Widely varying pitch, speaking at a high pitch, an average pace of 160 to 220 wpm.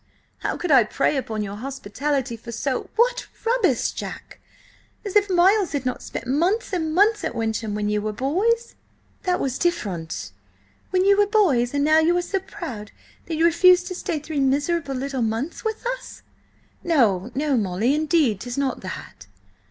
Yes: wide, 7.3 semitones; very high, 290 Hz; average, 175 wpm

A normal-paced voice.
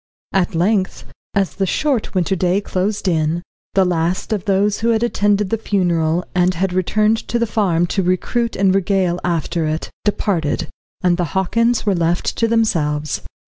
Yes: average, 170 wpm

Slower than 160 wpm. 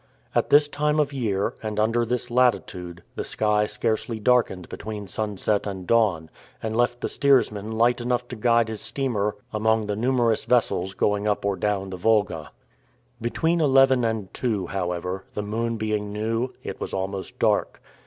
No: average, 165 wpm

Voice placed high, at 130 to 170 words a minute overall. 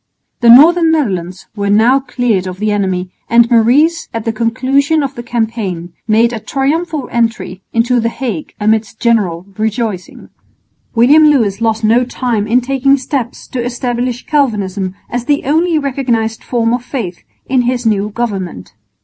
Yes: high, 235 Hz; average, 155 wpm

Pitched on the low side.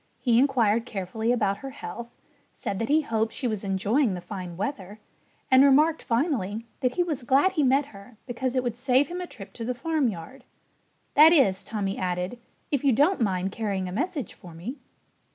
No: high, 240 Hz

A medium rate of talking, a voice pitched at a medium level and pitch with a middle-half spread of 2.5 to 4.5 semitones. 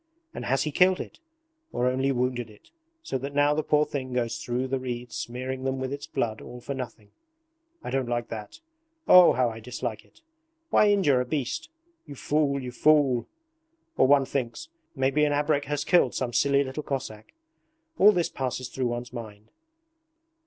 No: average, 180 wpm; low, 130 Hz; average, 2.9 semitones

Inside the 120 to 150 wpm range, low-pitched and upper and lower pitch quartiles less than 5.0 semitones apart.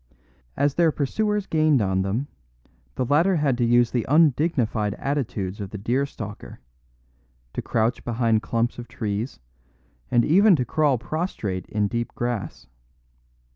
No: average, 140 wpm; low, 120 Hz; average, 5.3 semitones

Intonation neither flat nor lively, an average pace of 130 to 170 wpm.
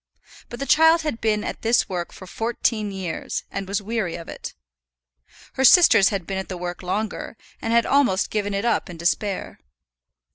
No: average, 3.7 semitones; average, 185 wpm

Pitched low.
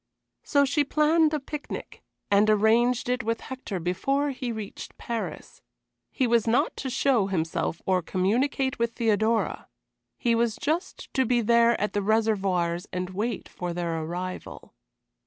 No: high, 230 Hz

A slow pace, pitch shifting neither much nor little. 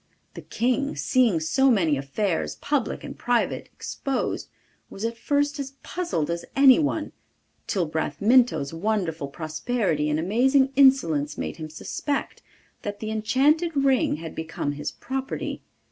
No: slow, 130 wpm; wide, 8.9 semitones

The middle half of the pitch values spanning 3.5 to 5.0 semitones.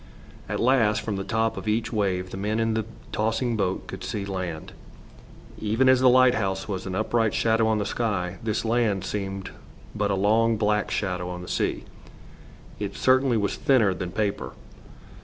No: average, 2.8 semitones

